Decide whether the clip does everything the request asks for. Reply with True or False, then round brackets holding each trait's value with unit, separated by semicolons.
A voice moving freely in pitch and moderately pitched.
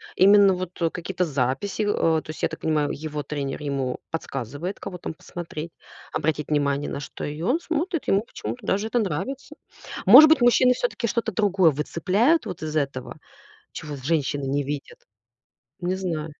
True (5.8 semitones; 165 Hz)